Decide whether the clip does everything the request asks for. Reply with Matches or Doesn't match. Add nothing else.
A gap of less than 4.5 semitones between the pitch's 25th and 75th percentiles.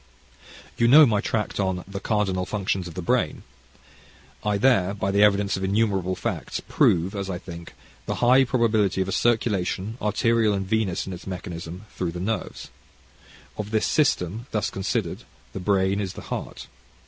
Matches